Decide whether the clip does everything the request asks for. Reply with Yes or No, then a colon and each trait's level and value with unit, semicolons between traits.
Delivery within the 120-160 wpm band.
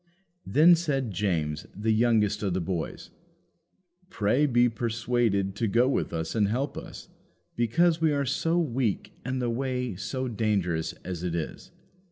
Yes: average, 155 wpm